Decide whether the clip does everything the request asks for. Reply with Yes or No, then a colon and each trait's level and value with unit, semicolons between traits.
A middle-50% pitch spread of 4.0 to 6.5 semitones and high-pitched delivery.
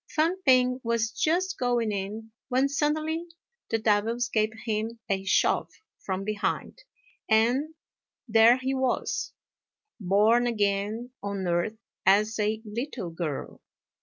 No: average, 3.5 semitones; high, 225 Hz